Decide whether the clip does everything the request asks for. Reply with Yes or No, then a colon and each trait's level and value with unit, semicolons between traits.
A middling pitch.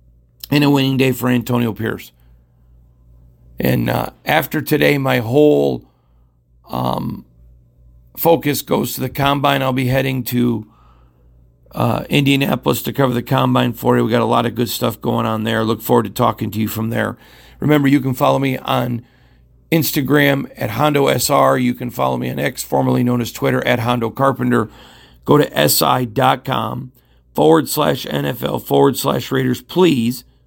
No: low, 120 Hz